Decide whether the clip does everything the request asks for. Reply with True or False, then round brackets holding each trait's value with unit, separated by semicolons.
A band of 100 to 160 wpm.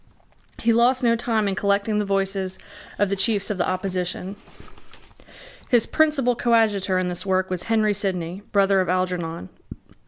True (155 wpm)